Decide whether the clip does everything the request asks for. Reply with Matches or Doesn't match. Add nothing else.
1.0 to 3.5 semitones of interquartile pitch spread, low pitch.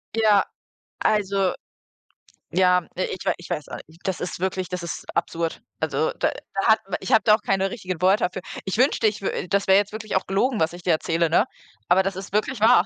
Doesn't match